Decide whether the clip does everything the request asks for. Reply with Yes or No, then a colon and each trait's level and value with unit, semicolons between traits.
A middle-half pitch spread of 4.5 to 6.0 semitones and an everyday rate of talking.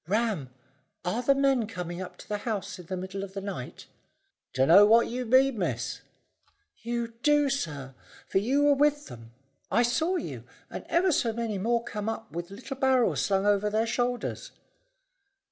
Yes: average, 5.0 semitones; average, 175 wpm